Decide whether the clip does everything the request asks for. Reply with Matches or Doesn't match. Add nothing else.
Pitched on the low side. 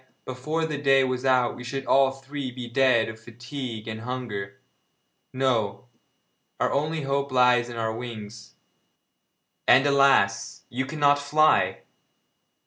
Matches